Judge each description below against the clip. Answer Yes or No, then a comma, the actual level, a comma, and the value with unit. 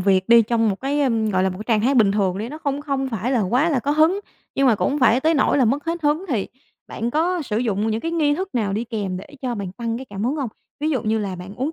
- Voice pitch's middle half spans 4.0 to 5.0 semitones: No, wide, 5.5 semitones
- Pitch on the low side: No, high, 240 Hz